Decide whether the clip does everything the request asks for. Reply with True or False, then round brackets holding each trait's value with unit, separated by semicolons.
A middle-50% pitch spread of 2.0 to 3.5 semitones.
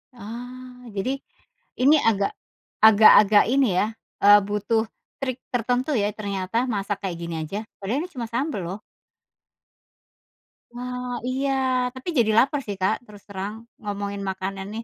False (3.9 semitones)